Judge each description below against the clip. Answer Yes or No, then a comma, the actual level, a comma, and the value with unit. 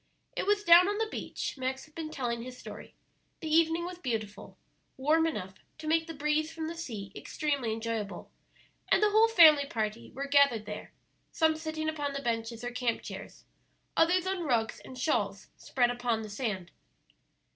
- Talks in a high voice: Yes, very high, 280 Hz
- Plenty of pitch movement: Yes, wide, 5.9 semitones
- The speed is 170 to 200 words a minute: Yes, average, 180 wpm